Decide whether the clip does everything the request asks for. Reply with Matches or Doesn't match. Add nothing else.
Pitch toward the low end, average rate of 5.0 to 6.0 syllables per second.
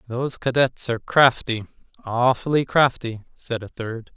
Doesn't match